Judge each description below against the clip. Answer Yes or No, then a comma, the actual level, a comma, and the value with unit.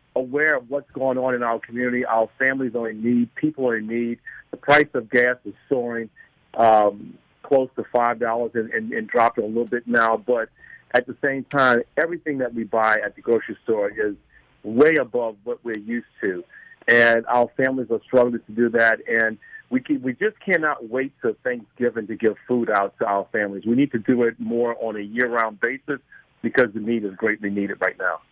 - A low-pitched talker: Yes, low, 120 Hz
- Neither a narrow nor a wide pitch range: Yes, average, 3.5 semitones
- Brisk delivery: Yes, fast, 210 wpm